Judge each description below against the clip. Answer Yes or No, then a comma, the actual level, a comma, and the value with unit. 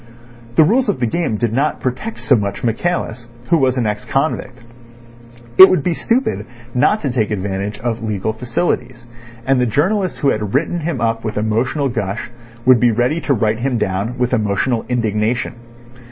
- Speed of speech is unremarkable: Yes, average, 180 wpm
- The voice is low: Yes, low, 125 Hz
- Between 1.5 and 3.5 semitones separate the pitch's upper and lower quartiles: No, average, 4.3 semitones